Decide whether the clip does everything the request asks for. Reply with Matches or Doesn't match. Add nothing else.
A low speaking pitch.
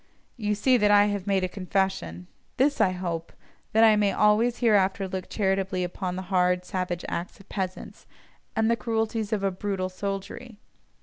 Doesn't match